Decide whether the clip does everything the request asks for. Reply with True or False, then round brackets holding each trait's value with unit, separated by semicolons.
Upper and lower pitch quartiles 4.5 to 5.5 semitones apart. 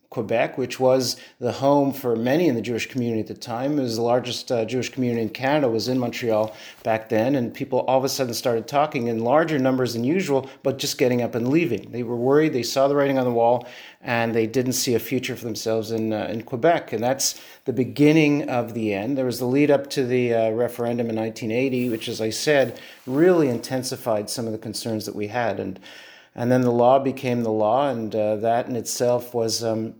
False (2.6 semitones)